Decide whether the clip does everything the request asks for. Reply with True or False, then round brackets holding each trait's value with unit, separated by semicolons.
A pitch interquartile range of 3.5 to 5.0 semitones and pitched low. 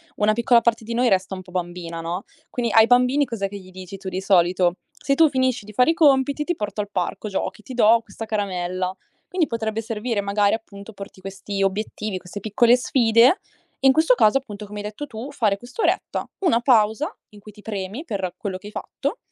False (4.0 semitones; 215 Hz)